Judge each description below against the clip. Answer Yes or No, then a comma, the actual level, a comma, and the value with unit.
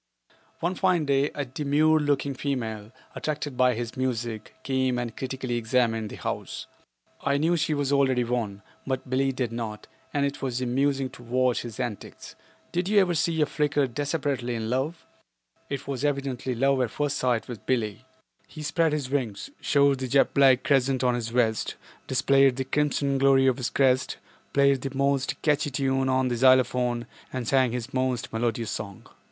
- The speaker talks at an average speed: Yes, average, 175 wpm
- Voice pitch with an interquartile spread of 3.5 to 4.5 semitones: No, narrow, 2.5 semitones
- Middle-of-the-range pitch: No, low, 130 Hz